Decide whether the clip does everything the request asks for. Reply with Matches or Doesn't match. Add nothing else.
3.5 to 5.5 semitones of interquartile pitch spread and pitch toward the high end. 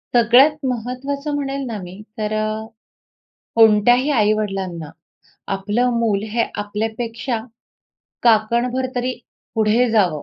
Doesn't match